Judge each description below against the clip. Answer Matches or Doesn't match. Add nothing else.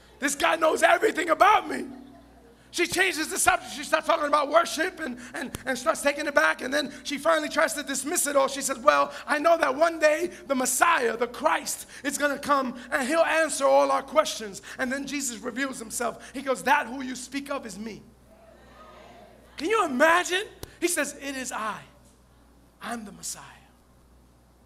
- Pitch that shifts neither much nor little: Matches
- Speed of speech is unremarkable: Matches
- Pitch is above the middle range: Matches